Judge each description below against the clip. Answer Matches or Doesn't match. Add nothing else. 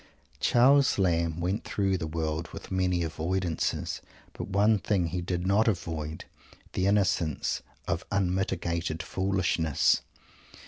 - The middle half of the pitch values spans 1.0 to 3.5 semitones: Matches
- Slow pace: Matches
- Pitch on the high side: Doesn't match